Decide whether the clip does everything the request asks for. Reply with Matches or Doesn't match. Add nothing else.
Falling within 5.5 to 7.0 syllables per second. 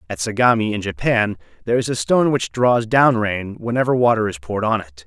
Matches